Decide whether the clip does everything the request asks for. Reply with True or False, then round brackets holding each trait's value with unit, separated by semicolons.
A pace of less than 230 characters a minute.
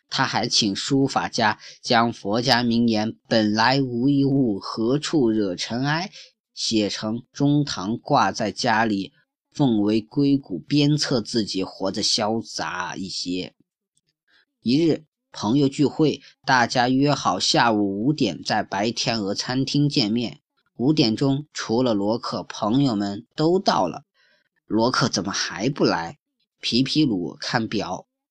True (190 characters per minute)